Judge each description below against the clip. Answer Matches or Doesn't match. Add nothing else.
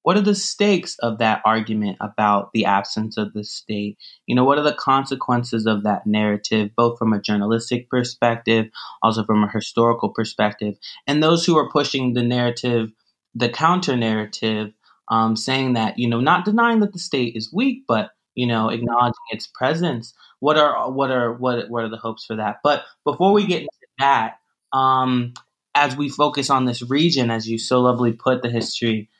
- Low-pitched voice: Matches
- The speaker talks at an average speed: Matches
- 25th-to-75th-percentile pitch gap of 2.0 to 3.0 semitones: Doesn't match